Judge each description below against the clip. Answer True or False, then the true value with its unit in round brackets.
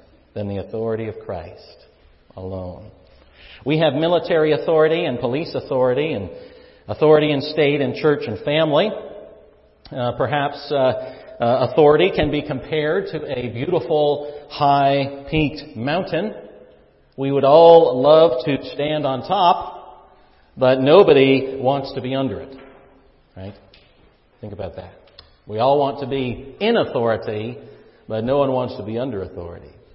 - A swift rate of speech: False (140 wpm)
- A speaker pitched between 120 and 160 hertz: True (140 Hz)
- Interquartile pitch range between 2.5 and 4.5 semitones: True (3.4 semitones)